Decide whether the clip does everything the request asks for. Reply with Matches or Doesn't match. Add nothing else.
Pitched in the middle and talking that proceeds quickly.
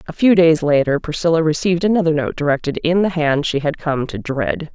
Matches